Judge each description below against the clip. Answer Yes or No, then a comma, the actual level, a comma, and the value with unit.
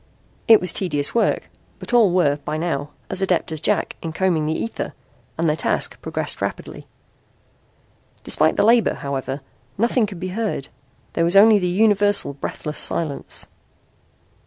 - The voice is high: No, medium, 175 Hz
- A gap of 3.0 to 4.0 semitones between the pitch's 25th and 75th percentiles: No, average, 5.1 semitones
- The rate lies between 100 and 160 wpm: Yes, average, 155 wpm